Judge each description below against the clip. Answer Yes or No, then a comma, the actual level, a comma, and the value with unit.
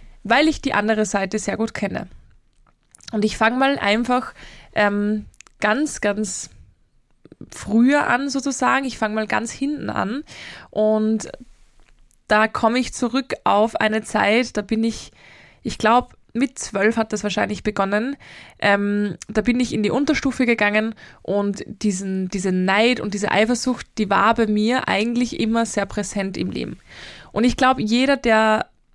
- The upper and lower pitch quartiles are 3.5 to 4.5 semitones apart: No, average, 3.1 semitones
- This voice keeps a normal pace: Yes, average, 155 wpm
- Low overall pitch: No, high, 220 Hz